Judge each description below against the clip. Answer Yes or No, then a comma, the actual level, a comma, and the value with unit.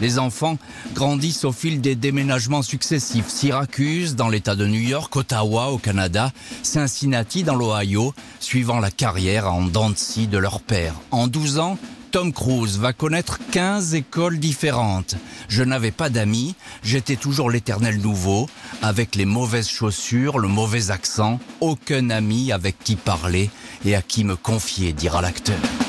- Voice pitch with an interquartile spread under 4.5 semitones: No, average, 4.8 semitones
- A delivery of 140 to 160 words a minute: Yes, average, 150 wpm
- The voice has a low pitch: Yes, low, 120 Hz